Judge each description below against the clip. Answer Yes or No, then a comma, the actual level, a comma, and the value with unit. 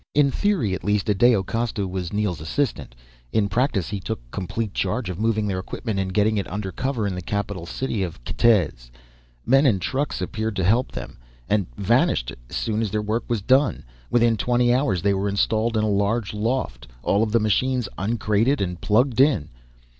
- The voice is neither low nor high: No, low, 105 Hz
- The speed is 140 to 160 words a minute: No, average, 190 wpm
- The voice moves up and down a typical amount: Yes, average, 3.5 semitones